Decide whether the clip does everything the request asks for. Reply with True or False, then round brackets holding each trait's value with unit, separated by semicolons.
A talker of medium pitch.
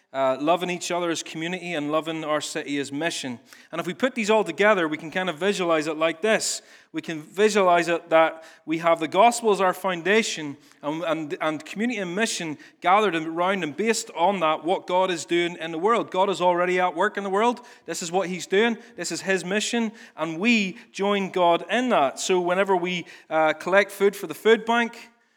True (180 Hz)